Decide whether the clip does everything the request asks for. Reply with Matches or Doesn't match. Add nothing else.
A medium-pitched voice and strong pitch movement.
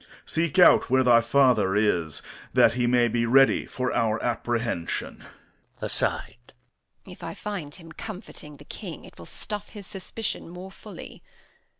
Doesn't match